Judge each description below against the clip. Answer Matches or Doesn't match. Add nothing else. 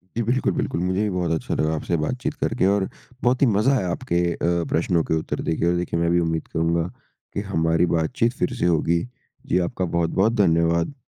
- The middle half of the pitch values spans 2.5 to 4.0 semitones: Matches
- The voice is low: Matches